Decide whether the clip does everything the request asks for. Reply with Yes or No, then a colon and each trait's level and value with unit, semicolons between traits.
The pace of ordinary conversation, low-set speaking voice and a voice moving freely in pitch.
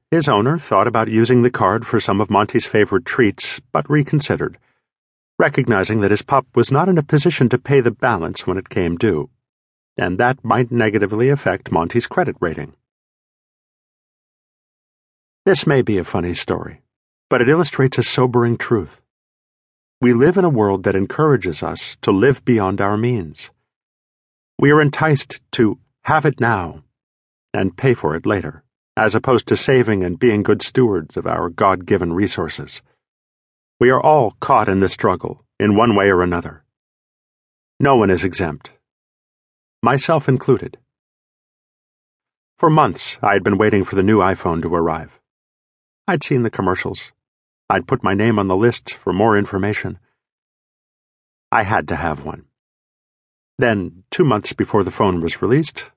Yes: average, 160 wpm; low, 110 Hz; wide, 5.8 semitones